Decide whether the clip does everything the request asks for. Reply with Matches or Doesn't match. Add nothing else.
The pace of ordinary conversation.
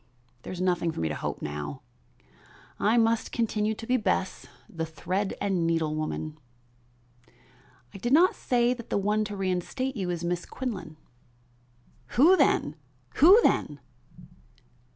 Matches